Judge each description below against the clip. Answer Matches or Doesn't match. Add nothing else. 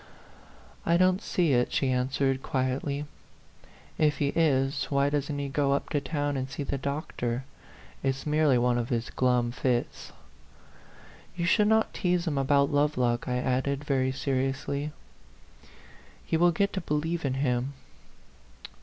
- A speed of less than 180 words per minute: Matches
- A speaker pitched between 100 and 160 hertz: Matches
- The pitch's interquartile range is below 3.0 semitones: Matches